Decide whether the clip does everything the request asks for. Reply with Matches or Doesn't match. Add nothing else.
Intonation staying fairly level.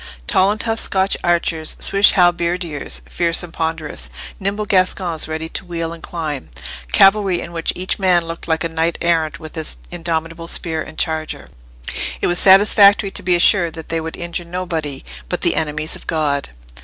Matches